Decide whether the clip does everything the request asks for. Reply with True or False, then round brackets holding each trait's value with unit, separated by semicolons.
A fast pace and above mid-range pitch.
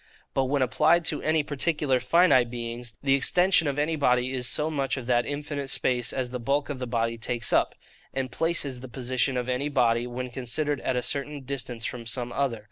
False (210 wpm; 130 Hz)